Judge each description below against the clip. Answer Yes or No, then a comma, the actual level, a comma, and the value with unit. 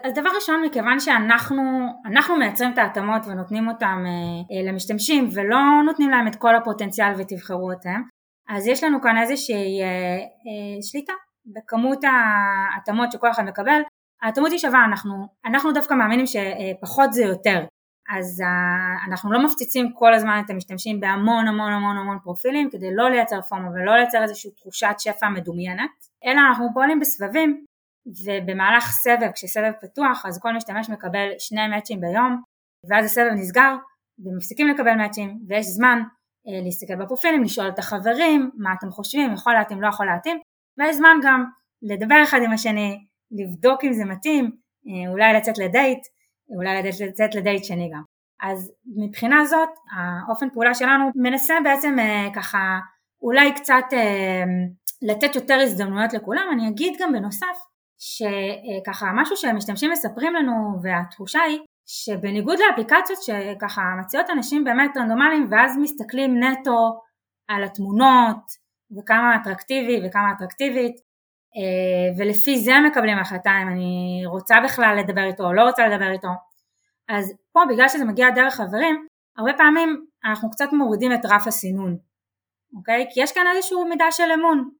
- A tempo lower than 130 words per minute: No, fast, 150 wpm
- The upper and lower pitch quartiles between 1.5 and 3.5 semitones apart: No, average, 5.1 semitones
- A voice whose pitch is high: Yes, high, 225 Hz